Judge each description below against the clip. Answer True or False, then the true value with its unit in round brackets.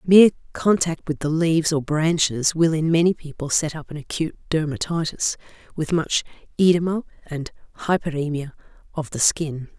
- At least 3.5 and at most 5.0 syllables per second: False (5.3 syllables/s)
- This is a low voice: False (160 Hz)